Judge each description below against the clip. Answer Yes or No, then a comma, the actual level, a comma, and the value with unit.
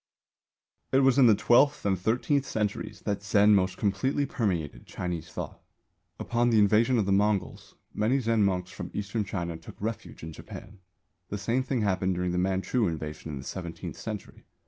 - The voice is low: Yes, low, 100 Hz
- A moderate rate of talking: Yes, average, 175 wpm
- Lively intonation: No, average, 3.9 semitones